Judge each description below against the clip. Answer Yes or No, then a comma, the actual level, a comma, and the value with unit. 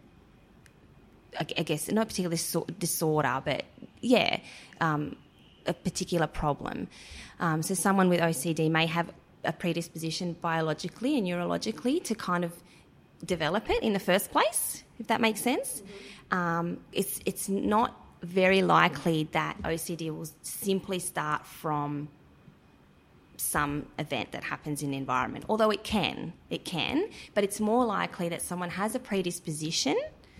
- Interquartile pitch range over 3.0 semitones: Yes, average, 3.6 semitones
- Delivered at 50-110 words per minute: No, average, 140 wpm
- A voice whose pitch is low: No, medium, 175 Hz